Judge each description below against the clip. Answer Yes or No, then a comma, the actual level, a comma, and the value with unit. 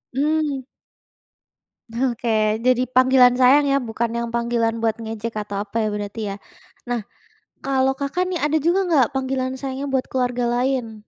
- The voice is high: Yes, very high, 255 Hz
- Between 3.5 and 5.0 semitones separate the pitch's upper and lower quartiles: No, average, 2.8 semitones